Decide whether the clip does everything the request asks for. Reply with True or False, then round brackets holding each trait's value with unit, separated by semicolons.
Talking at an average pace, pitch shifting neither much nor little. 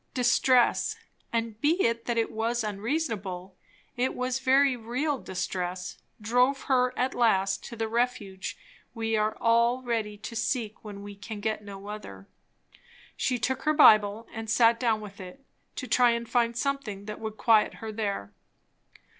True (160 wpm; 3.1 semitones)